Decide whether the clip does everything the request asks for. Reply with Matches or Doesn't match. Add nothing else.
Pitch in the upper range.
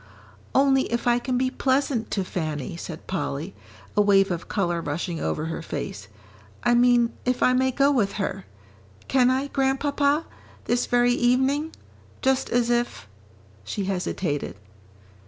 Matches